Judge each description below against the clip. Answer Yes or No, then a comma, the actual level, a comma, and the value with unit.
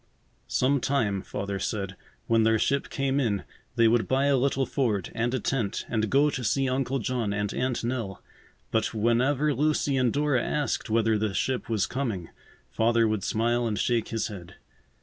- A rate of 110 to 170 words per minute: No, average, 180 wpm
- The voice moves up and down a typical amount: Yes, average, 3.7 semitones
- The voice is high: No, low, 120 Hz